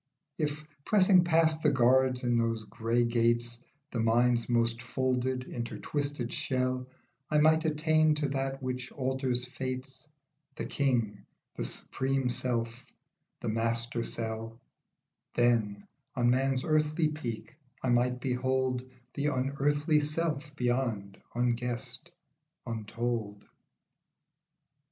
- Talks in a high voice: No, low, 125 Hz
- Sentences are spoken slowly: Yes, slow, 110 wpm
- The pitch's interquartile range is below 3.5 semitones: Yes, average, 3.1 semitones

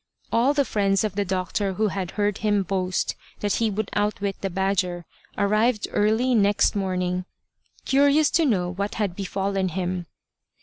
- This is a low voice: No, high, 200 Hz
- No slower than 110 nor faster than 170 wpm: Yes, average, 160 wpm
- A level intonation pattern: Yes, narrow, 2.3 semitones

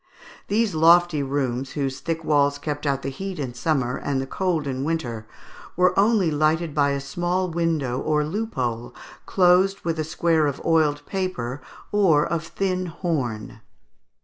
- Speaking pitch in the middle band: Yes, medium, 155 Hz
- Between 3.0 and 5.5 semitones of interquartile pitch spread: Yes, average, 4.1 semitones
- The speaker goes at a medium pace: Yes, average, 155 wpm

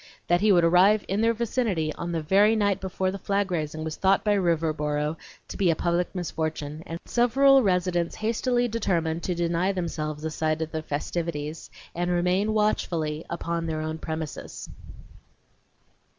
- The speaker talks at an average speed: Yes, average, 165 wpm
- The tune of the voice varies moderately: Yes, average, 3.9 semitones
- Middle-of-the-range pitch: Yes, medium, 175 Hz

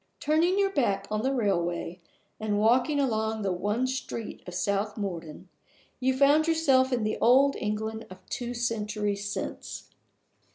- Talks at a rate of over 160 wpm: No, average, 150 wpm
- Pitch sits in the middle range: No, high, 220 Hz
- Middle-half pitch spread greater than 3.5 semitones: Yes, average, 4.4 semitones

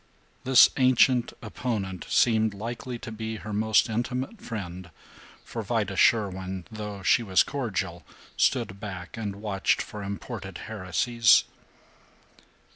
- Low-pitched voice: Yes, low, 110 Hz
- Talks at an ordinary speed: No, slow, 120 wpm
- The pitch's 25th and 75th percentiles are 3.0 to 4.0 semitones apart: Yes, average, 3.3 semitones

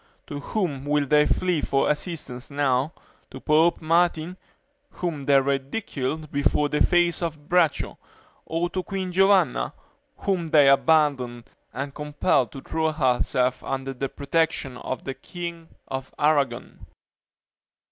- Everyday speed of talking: No, slow, 130 wpm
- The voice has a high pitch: No, medium, 150 Hz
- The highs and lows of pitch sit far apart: No, average, 3.6 semitones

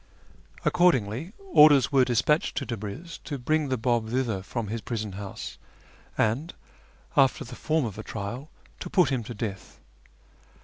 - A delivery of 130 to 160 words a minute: Yes, average, 150 wpm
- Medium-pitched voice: No, low, 120 Hz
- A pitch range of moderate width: Yes, average, 4.8 semitones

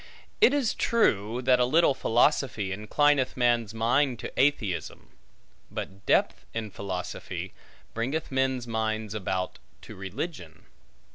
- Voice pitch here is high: No, low, 115 Hz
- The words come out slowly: Yes, slow, 120 wpm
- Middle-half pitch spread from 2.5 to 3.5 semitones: No, average, 4.6 semitones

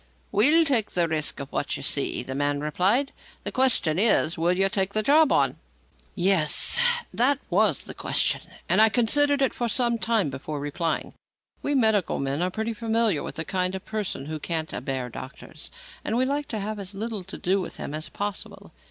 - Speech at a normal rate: Yes, average, 195 wpm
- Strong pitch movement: Yes, wide, 6.6 semitones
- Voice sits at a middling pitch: No, high, 195 Hz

